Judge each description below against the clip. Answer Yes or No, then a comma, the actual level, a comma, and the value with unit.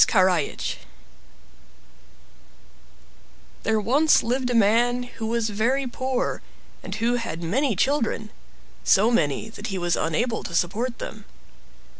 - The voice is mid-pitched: No, high, 225 Hz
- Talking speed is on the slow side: Yes, slow, 120 wpm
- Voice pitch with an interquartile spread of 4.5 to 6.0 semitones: No, average, 3.9 semitones